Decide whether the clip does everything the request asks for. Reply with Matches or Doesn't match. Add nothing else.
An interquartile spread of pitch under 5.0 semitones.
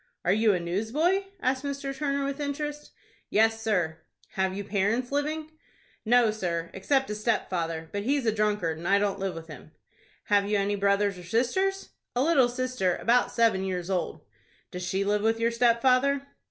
Doesn't match